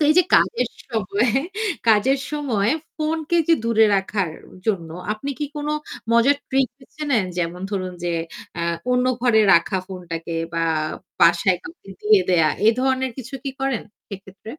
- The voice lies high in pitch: Yes, high, 220 Hz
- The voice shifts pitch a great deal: Yes, wide, 6.2 semitones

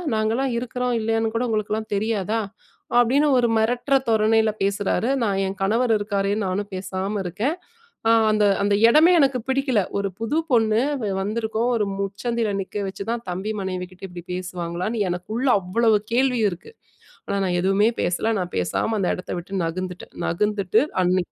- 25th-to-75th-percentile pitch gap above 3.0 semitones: Yes, average, 3.4 semitones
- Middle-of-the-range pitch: No, high, 215 Hz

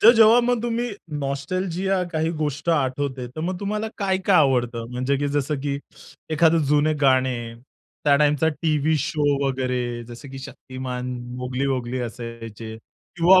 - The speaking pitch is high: No, medium, 140 Hz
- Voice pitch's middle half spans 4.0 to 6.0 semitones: Yes, average, 4.8 semitones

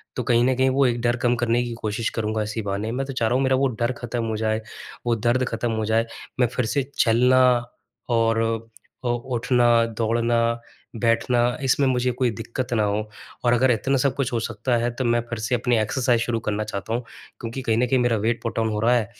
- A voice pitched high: No, low, 120 Hz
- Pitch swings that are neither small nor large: No, narrow, 1.8 semitones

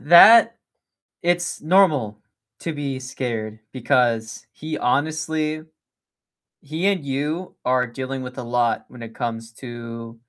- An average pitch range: Yes, average, 5.0 semitones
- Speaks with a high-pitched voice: No, low, 130 Hz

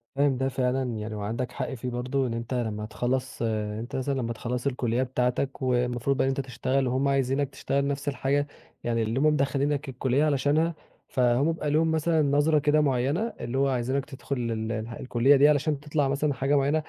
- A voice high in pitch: No, low, 135 Hz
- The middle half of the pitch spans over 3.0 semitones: No, average, 2.7 semitones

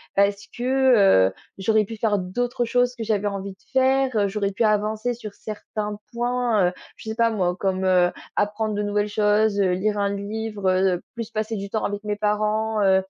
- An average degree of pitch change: No, narrow, 1.9 semitones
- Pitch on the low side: No, high, 210 Hz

